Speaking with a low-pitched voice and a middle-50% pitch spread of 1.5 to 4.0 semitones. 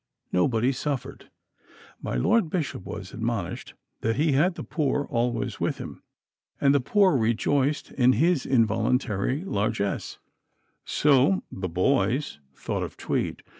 No: low, 130 Hz; average, 4.8 semitones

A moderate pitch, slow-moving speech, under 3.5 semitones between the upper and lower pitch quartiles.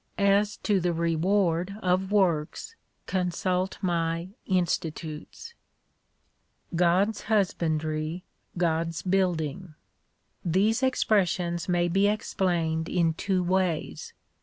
Yes: medium, 180 Hz; slow, 85 wpm; average, 2.7 semitones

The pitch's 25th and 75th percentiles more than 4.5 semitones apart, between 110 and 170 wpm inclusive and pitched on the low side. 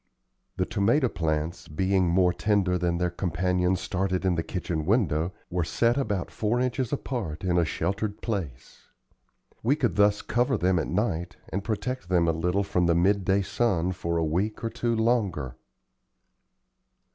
No: average, 3.8 semitones; average, 160 wpm; very low, 95 Hz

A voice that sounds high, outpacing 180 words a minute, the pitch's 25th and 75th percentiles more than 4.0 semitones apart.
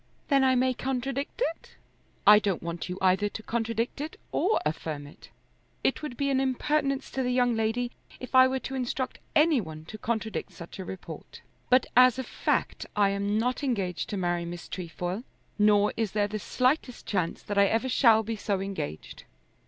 Yes: high, 225 Hz; average, 190 wpm; average, 4.9 semitones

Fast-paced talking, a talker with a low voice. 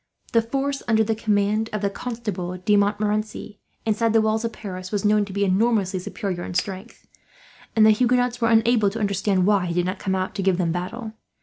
No: fast, 210 wpm; high, 210 Hz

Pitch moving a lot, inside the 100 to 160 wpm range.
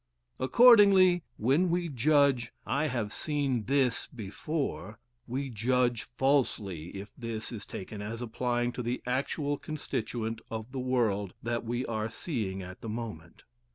No: average, 4.1 semitones; average, 140 wpm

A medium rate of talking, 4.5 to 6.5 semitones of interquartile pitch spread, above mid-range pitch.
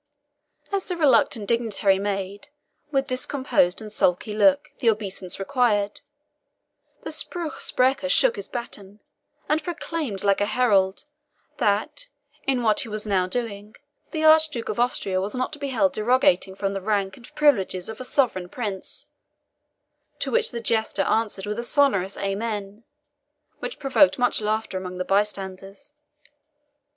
Yes: average, 145 wpm; wide, 5.4 semitones; high, 220 Hz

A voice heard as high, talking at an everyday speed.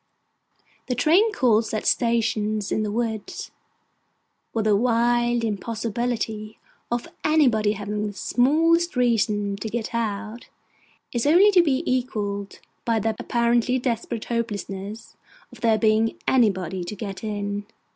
No: high, 225 Hz; slow, 125 wpm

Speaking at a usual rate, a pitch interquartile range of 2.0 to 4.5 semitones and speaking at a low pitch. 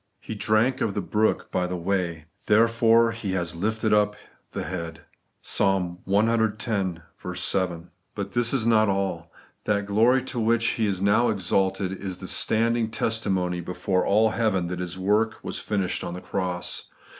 Yes: average, 160 wpm; average, 3.4 semitones; low, 100 Hz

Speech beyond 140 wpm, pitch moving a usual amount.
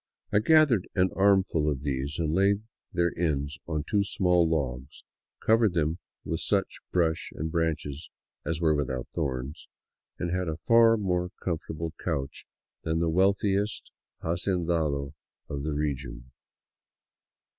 No: slow, 135 wpm; average, 4.1 semitones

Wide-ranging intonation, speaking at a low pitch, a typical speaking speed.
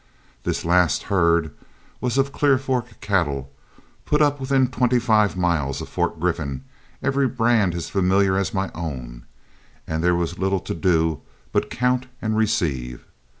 Yes: wide, 7.1 semitones; very low, 95 Hz; average, 150 wpm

